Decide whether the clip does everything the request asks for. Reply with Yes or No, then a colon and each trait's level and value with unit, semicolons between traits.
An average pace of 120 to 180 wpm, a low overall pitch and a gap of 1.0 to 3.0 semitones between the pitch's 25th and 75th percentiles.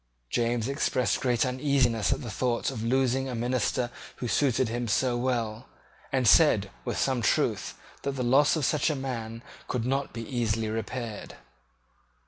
Yes: average, 160 wpm; low, 125 Hz; narrow, 2.4 semitones